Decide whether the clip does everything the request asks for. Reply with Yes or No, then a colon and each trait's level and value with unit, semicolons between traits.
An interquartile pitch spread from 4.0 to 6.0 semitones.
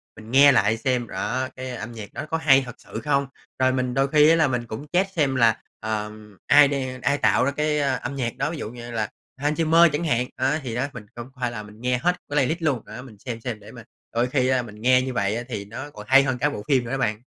No: average, 3.6 semitones